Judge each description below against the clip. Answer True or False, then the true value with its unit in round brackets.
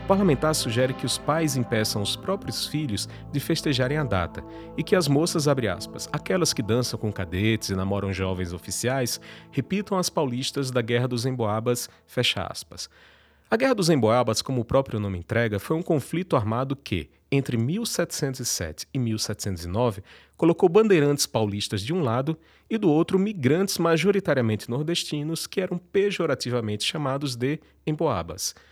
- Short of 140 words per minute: False (155 wpm)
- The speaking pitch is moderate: False (130 Hz)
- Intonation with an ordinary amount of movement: False (6.7 semitones)